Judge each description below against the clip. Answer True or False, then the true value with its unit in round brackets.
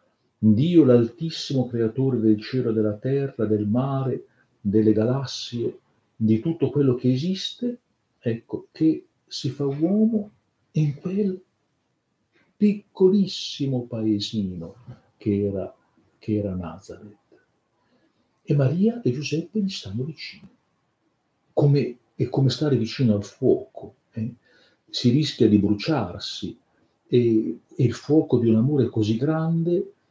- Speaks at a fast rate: False (115 wpm)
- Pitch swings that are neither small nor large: False (6.4 semitones)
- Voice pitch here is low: True (130 Hz)